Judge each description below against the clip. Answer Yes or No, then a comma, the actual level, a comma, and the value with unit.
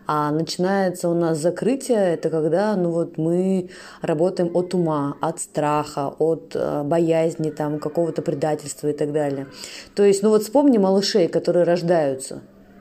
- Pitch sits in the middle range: Yes, medium, 165 Hz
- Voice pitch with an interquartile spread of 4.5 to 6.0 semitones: No, average, 2.9 semitones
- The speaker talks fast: No, average, 145 wpm